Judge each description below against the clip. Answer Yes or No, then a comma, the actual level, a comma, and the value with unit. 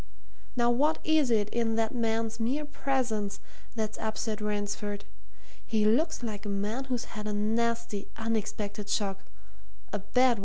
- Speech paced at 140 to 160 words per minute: Yes, average, 150 wpm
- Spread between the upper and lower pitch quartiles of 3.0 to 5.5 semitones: No, narrow, 2.5 semitones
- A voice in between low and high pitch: No, high, 225 Hz